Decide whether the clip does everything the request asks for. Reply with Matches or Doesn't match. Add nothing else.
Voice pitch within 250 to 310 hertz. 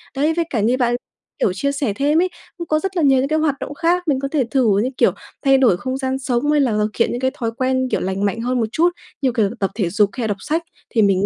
Matches